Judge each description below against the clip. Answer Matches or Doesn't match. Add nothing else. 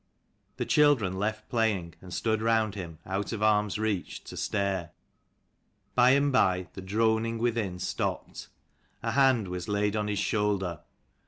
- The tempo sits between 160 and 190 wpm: Doesn't match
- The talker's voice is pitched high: Doesn't match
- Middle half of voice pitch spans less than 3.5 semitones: Matches